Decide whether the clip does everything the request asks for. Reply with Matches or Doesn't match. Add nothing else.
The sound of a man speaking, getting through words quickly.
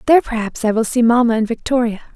Doesn't match